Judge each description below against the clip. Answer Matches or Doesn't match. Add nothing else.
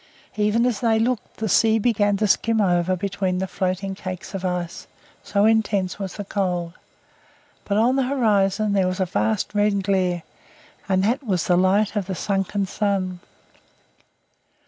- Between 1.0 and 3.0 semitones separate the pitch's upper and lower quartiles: Matches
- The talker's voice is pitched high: Matches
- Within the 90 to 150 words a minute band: Doesn't match